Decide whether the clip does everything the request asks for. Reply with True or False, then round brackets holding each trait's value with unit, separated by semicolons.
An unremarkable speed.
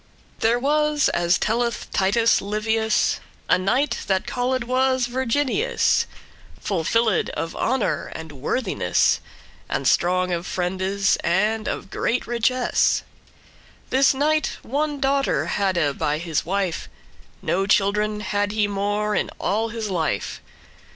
False (125 wpm)